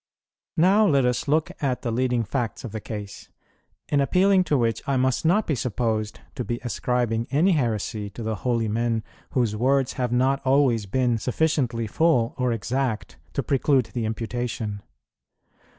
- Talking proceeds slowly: No, average, 165 wpm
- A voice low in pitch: Yes, low, 125 Hz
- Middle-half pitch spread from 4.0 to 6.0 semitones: No, average, 3.3 semitones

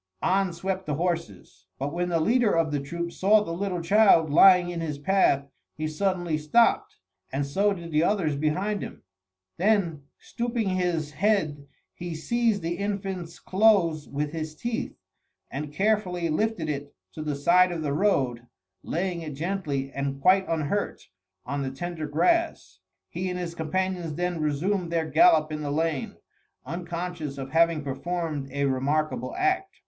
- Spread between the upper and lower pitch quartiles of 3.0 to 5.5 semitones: Yes, average, 4.2 semitones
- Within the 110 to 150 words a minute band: No, average, 160 wpm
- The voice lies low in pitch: No, medium, 170 Hz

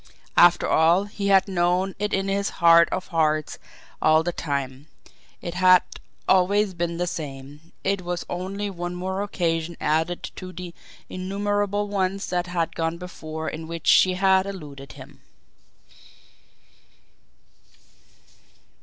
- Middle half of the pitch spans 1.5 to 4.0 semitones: Yes, average, 2.8 semitones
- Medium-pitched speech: Yes, medium, 180 Hz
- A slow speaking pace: Yes, slow, 130 wpm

